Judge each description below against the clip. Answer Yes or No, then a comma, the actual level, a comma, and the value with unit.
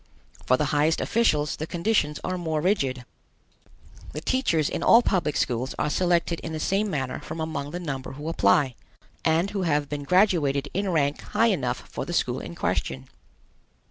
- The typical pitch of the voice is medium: Yes, medium, 160 Hz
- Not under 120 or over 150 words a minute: No, average, 175 wpm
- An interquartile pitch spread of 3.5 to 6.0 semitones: Yes, average, 4.1 semitones